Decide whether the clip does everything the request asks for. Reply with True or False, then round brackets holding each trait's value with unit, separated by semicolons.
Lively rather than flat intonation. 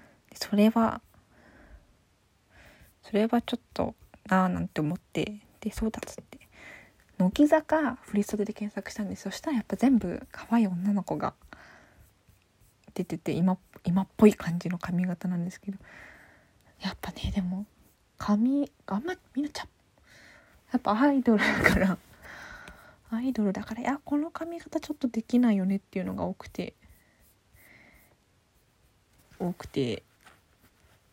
False (4.9 semitones)